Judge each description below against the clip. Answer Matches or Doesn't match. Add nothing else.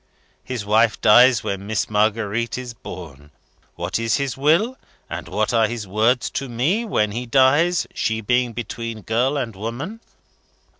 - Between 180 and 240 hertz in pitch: Doesn't match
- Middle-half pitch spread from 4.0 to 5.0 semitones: Doesn't match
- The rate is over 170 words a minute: Doesn't match